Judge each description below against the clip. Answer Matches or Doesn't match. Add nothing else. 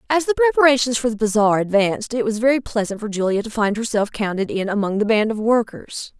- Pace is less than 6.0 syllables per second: Doesn't match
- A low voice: Doesn't match